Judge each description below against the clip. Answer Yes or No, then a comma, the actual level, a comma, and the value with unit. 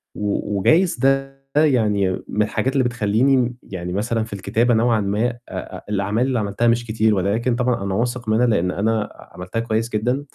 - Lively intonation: No, average, 3.1 semitones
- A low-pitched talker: Yes, low, 115 Hz